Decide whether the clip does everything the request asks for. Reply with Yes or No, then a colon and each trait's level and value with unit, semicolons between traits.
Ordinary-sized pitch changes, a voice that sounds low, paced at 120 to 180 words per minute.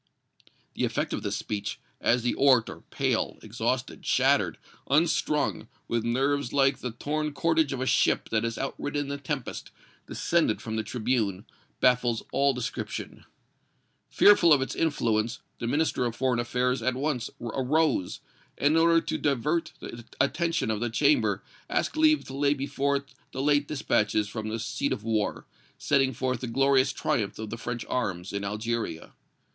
Yes: average, 3.9 semitones; low, 130 Hz; average, 160 wpm